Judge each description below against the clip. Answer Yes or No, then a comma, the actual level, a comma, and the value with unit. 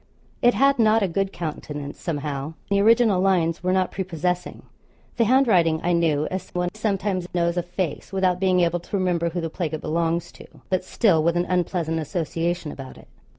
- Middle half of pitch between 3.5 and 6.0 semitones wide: No, narrow, 2.5 semitones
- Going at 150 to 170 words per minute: No, average, 190 wpm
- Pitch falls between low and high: Yes, medium, 175 Hz